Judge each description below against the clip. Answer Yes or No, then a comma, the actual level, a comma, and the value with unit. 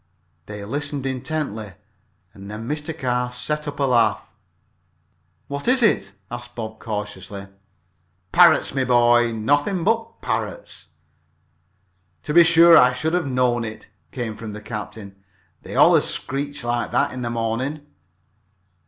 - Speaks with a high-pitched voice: No, low, 125 Hz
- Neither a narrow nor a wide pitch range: Yes, average, 4.6 semitones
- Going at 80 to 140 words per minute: Yes, slow, 135 wpm